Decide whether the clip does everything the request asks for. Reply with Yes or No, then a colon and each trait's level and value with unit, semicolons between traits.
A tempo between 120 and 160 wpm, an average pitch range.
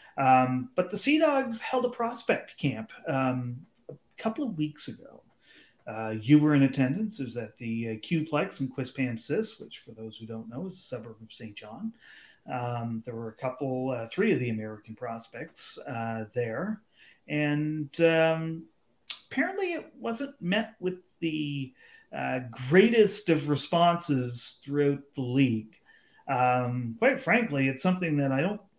No: average, 155 wpm; wide, 6.8 semitones